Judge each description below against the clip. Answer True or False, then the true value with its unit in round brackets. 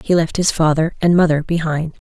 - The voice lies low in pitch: False (160 Hz)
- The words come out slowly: False (205 wpm)